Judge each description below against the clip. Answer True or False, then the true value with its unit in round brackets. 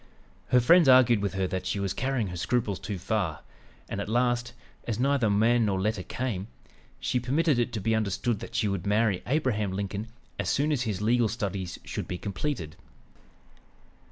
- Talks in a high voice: False (110 Hz)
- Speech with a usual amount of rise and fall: True (3.8 semitones)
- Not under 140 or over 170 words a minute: False (185 wpm)